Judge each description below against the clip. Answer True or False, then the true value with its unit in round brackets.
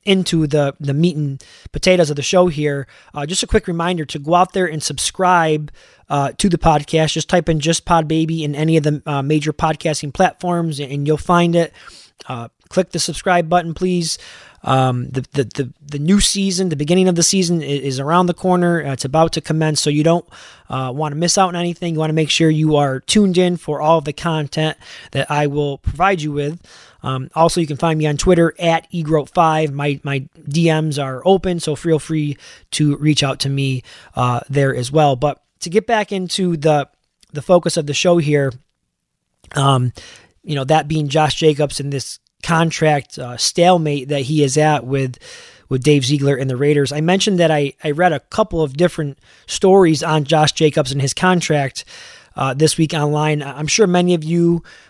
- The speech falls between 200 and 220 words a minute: True (205 wpm)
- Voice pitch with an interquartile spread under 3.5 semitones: True (3.0 semitones)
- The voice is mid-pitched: True (155 Hz)